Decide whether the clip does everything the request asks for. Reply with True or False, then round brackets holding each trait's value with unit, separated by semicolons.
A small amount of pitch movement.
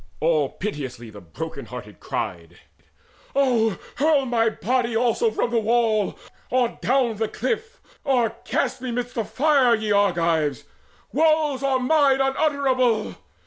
False (4.4 semitones)